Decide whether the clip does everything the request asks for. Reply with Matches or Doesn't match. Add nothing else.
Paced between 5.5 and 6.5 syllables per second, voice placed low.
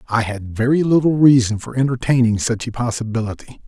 Matches